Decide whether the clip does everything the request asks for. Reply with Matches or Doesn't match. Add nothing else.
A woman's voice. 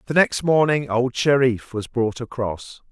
Doesn't match